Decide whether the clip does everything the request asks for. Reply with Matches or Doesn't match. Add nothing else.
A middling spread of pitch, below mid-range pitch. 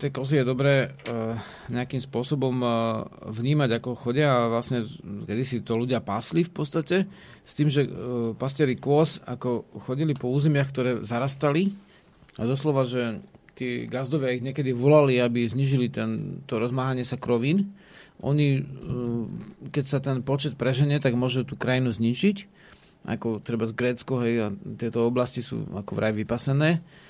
Matches